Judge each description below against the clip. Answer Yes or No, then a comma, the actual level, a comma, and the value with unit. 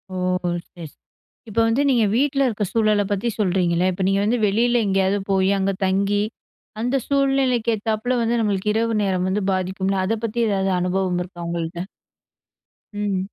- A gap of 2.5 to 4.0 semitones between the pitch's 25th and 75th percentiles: Yes, average, 3.4 semitones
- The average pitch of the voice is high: Yes, high, 205 Hz